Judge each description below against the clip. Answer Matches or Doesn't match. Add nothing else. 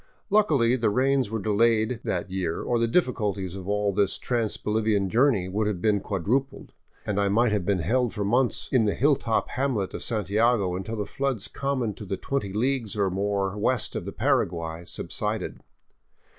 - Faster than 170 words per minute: Matches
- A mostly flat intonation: Doesn't match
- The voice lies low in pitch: Matches